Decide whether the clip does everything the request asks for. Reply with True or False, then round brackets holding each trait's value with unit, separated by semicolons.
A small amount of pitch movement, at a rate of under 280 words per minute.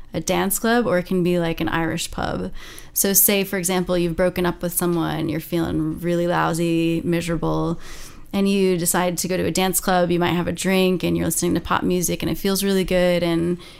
True (1.5 semitones; 220 wpm)